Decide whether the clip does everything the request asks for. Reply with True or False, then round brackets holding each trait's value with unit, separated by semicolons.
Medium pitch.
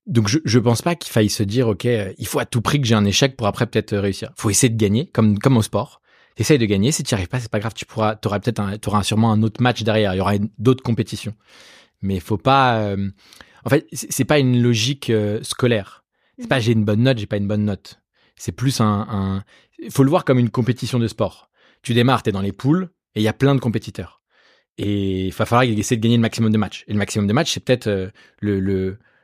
False (110 Hz)